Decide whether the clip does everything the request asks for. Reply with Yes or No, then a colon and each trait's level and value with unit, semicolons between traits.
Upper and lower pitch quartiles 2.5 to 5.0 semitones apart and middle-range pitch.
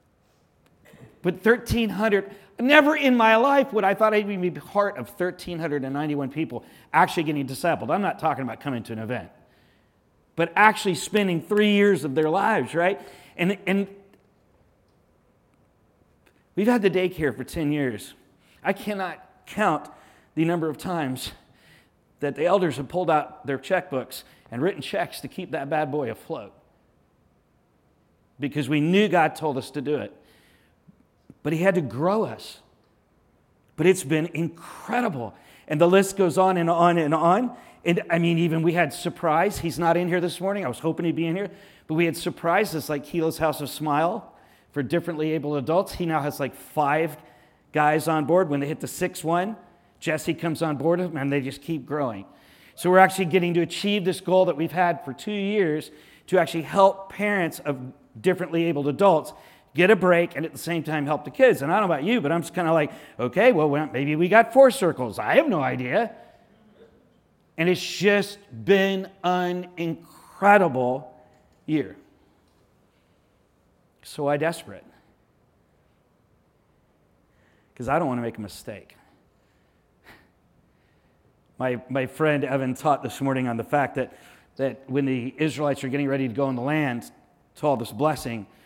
Yes: average, 4.5 semitones; medium, 165 Hz